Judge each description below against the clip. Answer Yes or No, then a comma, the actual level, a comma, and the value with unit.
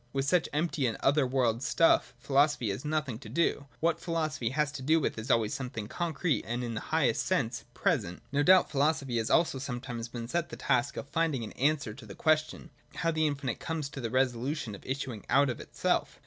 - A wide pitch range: No, average, 4.3 semitones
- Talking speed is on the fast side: Yes, fast, 210 wpm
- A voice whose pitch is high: No, medium, 140 Hz